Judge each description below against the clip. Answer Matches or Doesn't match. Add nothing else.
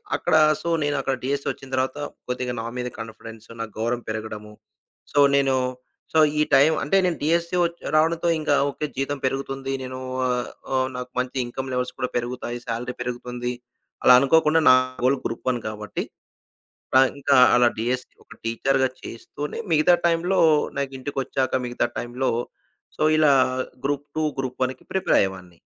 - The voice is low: Matches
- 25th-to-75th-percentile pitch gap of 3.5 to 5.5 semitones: Doesn't match